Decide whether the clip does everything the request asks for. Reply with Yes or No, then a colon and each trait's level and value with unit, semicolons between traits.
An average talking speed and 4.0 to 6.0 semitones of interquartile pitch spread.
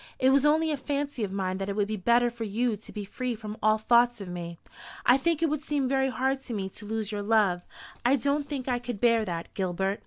No: fast, 255 wpm; average, 4.7 semitones